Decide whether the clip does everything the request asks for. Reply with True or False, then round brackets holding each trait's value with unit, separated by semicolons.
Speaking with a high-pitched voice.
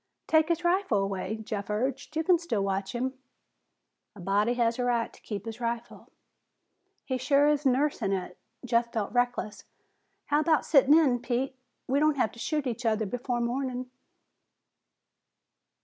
True (245 Hz)